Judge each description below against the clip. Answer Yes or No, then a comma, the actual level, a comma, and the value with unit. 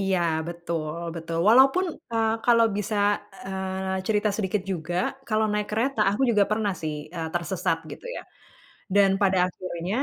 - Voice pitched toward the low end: No, high, 195 Hz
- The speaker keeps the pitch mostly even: No, average, 3.8 semitones